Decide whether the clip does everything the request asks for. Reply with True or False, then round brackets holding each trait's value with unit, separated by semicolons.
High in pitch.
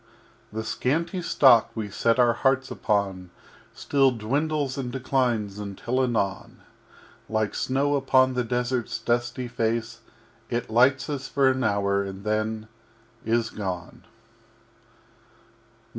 False (120 Hz)